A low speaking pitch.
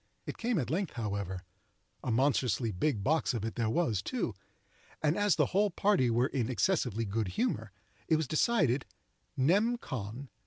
Yes: low, 130 Hz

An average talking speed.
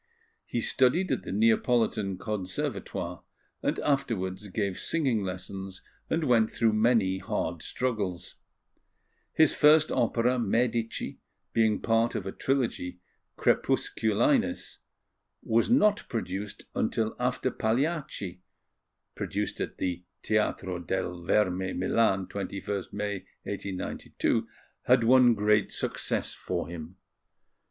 No: slow, 105 wpm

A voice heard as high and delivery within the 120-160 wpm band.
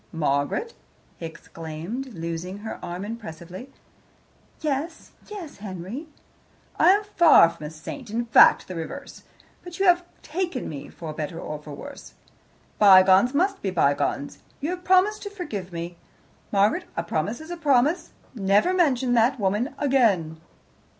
Yes: high, 220 Hz; average, 145 wpm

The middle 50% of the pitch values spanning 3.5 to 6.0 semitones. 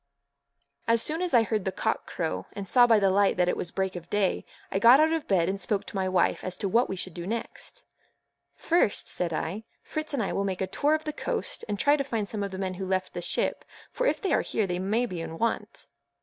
Yes: average, 4.4 semitones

